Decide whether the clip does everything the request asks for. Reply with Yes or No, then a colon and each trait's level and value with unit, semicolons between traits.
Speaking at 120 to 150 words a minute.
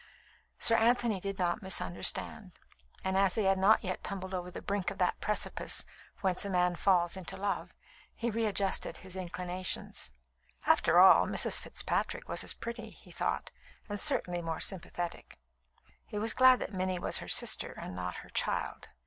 No: average, 165 wpm